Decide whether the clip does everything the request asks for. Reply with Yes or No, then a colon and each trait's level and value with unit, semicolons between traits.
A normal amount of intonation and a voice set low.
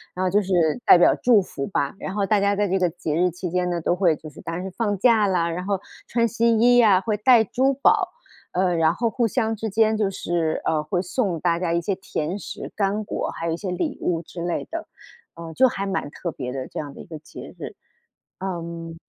No: average, 4.0 semitones; medium, 185 Hz